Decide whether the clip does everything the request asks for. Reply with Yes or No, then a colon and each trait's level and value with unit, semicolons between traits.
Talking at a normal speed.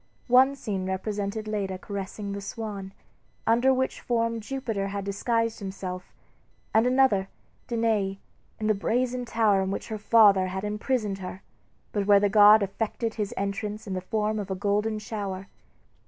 Yes: average, 155 wpm